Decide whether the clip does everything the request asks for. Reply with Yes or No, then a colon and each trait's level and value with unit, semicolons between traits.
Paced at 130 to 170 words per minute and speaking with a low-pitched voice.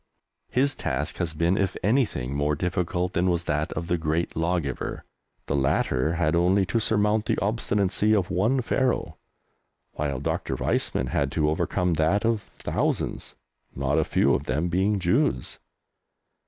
Yes: average, 155 wpm; very low, 85 Hz